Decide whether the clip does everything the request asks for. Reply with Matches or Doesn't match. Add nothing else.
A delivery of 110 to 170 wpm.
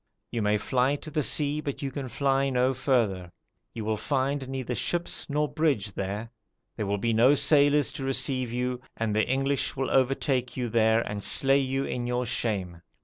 Doesn't match